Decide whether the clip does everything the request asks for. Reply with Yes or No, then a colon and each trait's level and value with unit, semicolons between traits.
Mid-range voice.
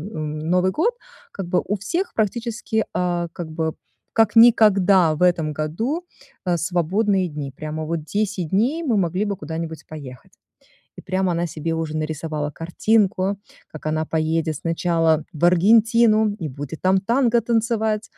Yes: medium, 180 Hz